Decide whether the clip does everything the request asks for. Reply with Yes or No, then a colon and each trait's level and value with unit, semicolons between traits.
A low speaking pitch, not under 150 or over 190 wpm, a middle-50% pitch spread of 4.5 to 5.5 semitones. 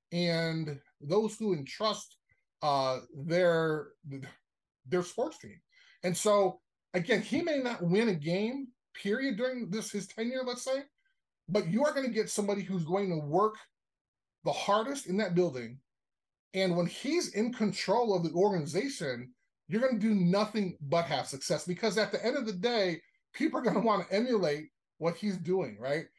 No: high, 195 Hz; average, 170 wpm; average, 4.8 semitones